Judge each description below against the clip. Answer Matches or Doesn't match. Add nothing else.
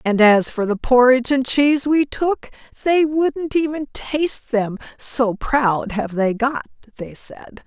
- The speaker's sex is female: Matches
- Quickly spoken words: Doesn't match